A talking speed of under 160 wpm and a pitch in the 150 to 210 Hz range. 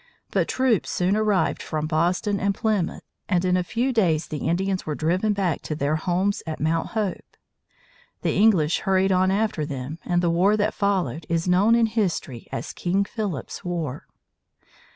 No: average, 175 wpm; medium, 185 Hz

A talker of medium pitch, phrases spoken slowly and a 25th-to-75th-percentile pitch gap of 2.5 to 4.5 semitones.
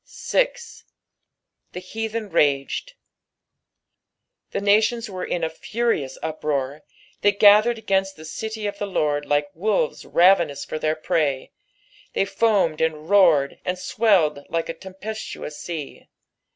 No: medium, 180 Hz; slow, 130 wpm; average, 5.2 semitones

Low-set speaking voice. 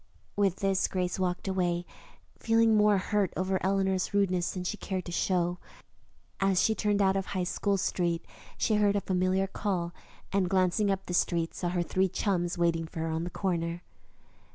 No: medium, 185 Hz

